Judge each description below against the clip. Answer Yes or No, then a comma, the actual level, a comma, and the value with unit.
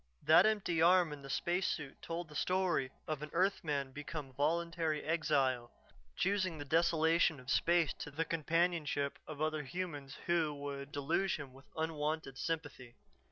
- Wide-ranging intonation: No, average, 3.1 semitones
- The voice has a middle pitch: Yes, medium, 155 Hz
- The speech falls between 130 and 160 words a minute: Yes, average, 150 wpm